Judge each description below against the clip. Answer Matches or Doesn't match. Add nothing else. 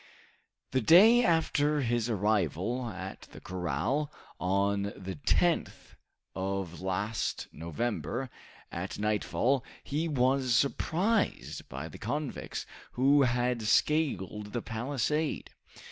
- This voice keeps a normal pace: Doesn't match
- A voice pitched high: Doesn't match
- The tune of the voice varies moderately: Doesn't match